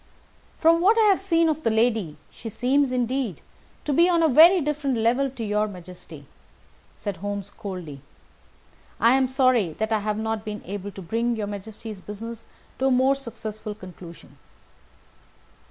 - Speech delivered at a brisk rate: No, average, 165 wpm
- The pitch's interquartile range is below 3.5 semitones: No, average, 4.8 semitones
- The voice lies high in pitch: Yes, high, 225 Hz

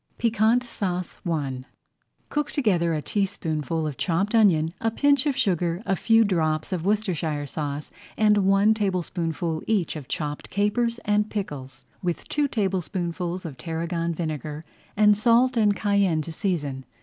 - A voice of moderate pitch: Yes, medium, 180 Hz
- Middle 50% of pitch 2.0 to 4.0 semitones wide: No, average, 4.8 semitones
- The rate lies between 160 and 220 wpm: No, average, 150 wpm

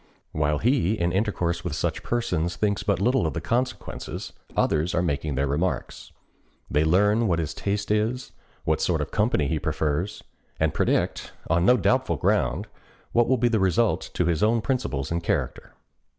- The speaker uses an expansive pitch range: Yes, wide, 5.8 semitones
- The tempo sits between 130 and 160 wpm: No, average, 175 wpm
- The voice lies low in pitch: Yes, very low, 90 Hz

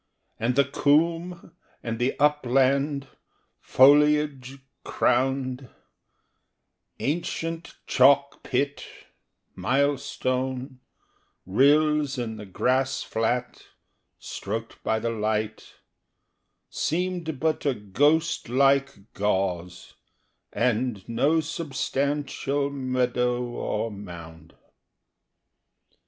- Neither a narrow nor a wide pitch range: Yes, average, 3.8 semitones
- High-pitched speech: No, low, 130 Hz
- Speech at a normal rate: No, slow, 75 wpm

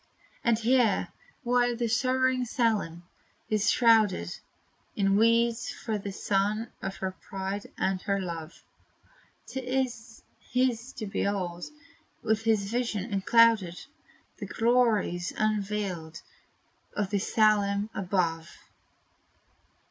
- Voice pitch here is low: No, high, 210 Hz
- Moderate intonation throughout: Yes, average, 3.2 semitones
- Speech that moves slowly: Yes, slow, 105 wpm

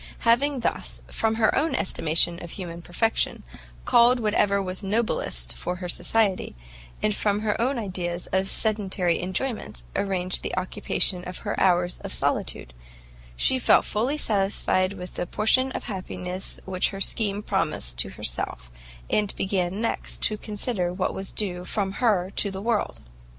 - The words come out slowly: No, average, 155 wpm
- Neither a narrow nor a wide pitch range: Yes, average, 3.3 semitones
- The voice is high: Yes, high, 195 Hz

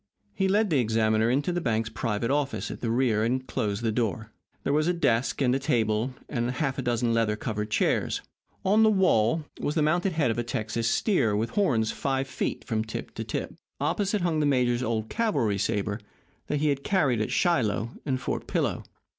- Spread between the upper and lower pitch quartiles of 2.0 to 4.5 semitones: No, average, 5.1 semitones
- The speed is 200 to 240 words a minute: Yes, fast, 205 wpm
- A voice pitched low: Yes, low, 125 Hz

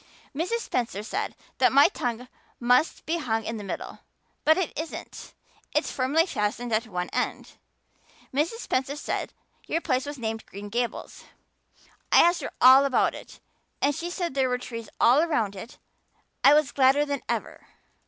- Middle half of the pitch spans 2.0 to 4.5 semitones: No, average, 4.9 semitones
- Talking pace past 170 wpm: No, average, 165 wpm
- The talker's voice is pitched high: Yes, very high, 260 Hz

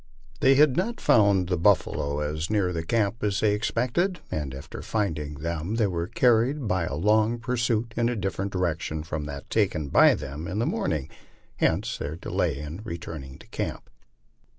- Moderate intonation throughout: No, wide, 6.7 semitones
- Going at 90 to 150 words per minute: No, average, 175 wpm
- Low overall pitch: Yes, very low, 95 Hz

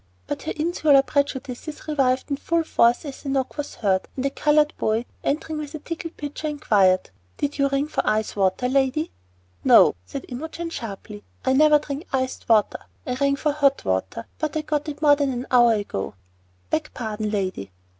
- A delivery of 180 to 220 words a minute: Yes, average, 185 wpm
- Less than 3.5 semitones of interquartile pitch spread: No, average, 4.6 semitones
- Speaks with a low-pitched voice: No, very high, 275 Hz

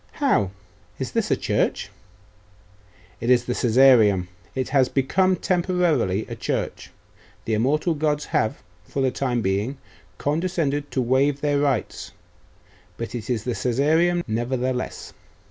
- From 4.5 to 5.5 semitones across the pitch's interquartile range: No, average, 4.1 semitones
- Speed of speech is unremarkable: No, slow, 130 wpm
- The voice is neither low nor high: No, low, 130 Hz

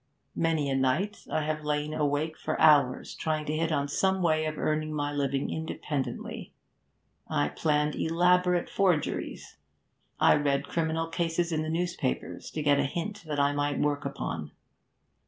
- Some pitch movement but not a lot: No, narrow, 2.2 semitones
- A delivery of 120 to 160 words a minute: Yes, average, 155 wpm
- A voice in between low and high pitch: Yes, medium, 155 Hz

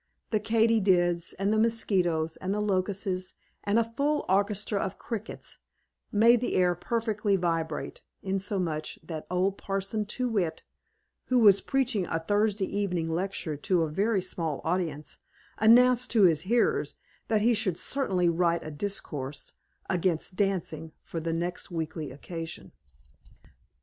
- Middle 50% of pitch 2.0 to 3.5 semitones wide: No, average, 4.4 semitones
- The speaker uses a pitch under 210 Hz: Yes, high, 190 Hz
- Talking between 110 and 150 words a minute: Yes, average, 140 wpm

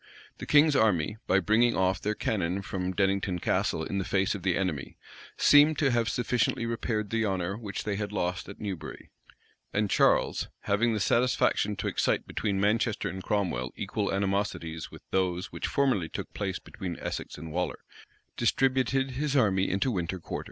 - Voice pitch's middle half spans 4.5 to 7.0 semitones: No, average, 3.8 semitones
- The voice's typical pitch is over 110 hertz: No, low, 100 Hz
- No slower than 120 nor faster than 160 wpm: No, average, 175 wpm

